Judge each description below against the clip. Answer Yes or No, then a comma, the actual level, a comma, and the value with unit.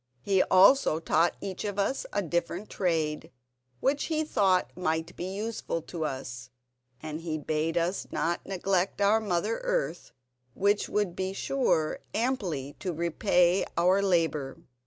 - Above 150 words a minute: No, average, 140 wpm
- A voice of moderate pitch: Yes, medium, 180 Hz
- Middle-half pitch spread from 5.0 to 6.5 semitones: No, average, 3.8 semitones